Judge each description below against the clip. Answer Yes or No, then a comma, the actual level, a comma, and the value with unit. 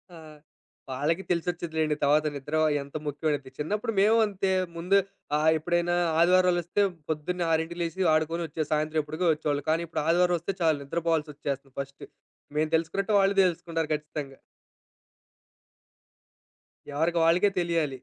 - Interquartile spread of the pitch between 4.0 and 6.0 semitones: No, narrow, 2.5 semitones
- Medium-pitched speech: Yes, medium, 160 Hz